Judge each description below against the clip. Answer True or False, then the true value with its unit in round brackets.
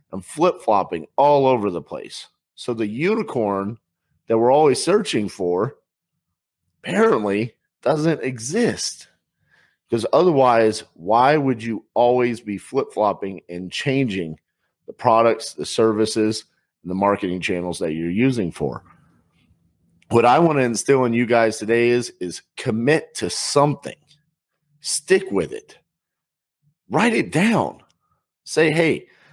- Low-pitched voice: True (120 Hz)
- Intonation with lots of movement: True (6.1 semitones)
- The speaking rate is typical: False (125 wpm)